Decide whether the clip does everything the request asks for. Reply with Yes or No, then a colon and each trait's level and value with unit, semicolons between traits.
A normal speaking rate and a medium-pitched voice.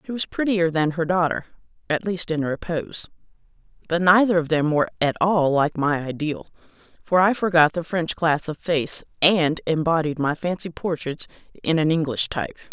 Yes: average, 175 wpm; medium, 165 Hz